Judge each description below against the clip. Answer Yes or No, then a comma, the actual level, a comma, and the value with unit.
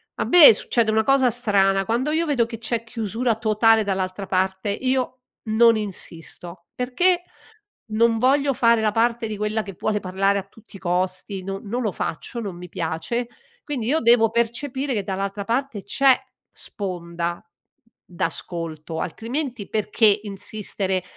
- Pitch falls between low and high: No, high, 215 Hz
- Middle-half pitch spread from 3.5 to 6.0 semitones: Yes, average, 3.8 semitones